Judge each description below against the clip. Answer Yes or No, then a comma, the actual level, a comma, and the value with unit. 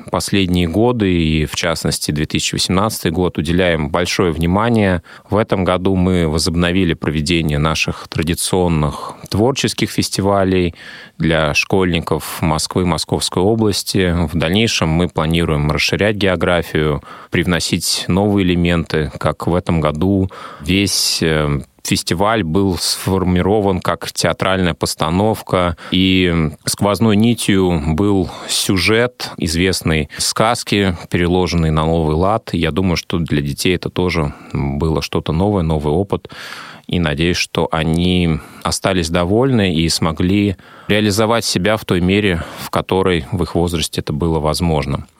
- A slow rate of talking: No, average, 120 wpm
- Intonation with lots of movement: No, average, 3.0 semitones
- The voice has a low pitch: Yes, very low, 90 Hz